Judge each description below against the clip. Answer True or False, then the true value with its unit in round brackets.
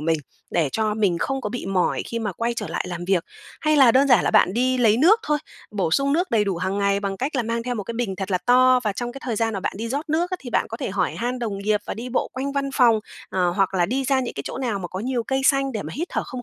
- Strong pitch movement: False (4.8 semitones)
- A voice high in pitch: True (230 Hz)